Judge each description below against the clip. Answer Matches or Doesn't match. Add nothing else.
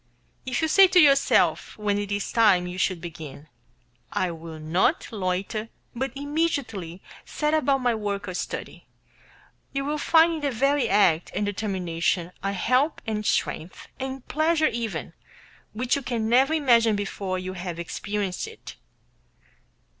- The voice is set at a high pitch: Matches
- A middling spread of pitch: Doesn't match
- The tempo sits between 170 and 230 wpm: Doesn't match